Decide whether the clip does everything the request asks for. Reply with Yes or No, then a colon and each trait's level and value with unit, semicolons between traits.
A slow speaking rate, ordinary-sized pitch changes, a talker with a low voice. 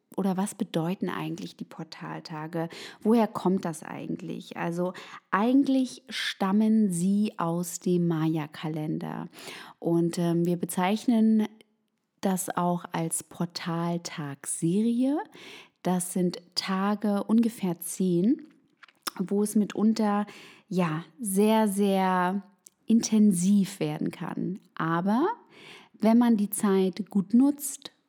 No: slow, 100 wpm; average, 3.9 semitones; high, 195 Hz